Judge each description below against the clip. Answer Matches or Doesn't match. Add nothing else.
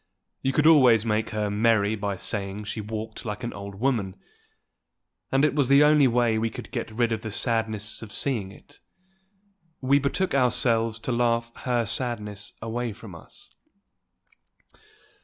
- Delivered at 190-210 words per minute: Doesn't match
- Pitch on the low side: Matches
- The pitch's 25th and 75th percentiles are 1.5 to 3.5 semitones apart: Matches